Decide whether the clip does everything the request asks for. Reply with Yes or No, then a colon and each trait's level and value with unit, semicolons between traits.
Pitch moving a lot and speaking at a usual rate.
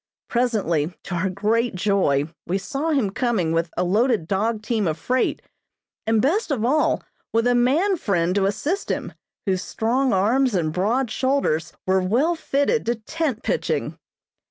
Yes: wide, 5.8 semitones; average, 160 wpm